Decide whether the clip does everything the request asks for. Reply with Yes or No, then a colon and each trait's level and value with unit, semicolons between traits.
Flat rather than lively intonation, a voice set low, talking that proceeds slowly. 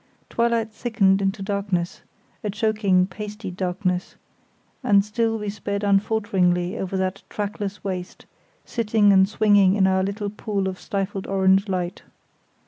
No: narrow, 1.8 semitones; high, 200 Hz; slow, 125 wpm